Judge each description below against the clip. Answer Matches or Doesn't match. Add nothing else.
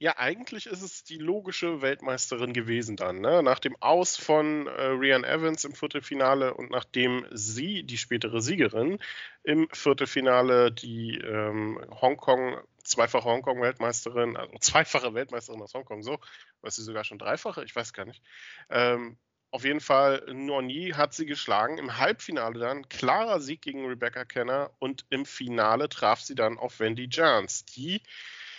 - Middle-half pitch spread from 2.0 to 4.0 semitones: Matches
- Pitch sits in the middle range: Doesn't match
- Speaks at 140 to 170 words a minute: Matches